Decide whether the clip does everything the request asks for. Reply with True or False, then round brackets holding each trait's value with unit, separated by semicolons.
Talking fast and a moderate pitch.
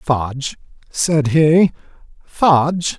False (80 wpm; 150 Hz)